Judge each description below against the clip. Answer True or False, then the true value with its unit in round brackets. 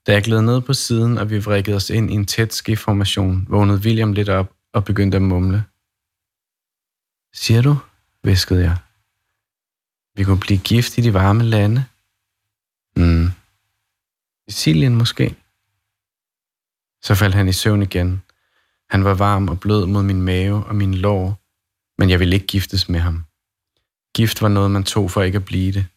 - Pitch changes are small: True (1.9 semitones)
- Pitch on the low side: True (100 Hz)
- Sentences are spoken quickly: False (165 wpm)